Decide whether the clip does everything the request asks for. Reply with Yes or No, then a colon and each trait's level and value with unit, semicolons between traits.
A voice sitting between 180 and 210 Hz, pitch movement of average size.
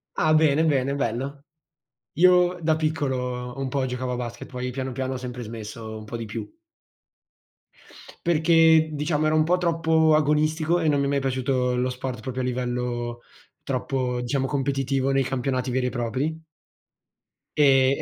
No: low, 135 Hz; average, 3.7 semitones